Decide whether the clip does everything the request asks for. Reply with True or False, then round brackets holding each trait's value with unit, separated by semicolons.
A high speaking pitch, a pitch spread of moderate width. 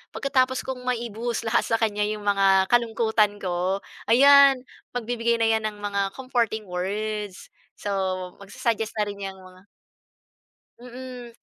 True (220 Hz; 3.1 semitones)